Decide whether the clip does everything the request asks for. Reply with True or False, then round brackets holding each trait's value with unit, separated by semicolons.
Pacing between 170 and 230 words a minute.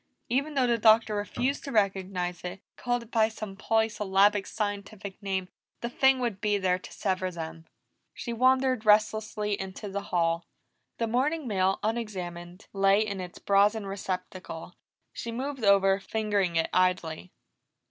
False (145 wpm)